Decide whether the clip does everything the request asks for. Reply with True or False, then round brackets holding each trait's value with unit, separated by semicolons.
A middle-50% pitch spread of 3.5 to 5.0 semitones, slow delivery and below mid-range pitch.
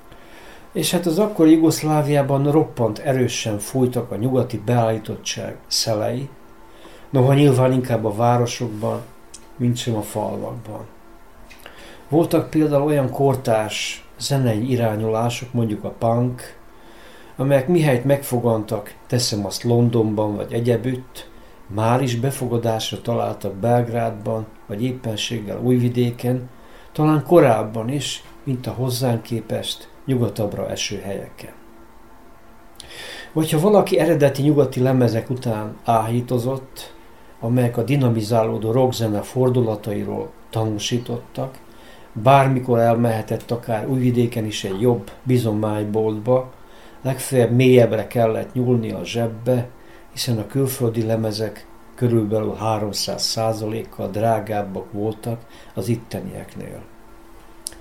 False (2.4 semitones; 100 wpm; 115 Hz)